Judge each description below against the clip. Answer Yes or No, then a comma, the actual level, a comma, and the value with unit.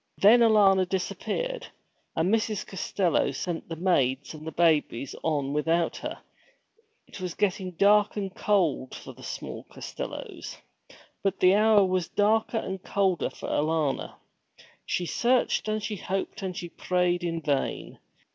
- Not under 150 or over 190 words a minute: No, average, 140 wpm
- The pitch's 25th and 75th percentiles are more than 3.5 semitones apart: Yes, average, 3.9 semitones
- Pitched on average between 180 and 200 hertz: Yes, medium, 185 Hz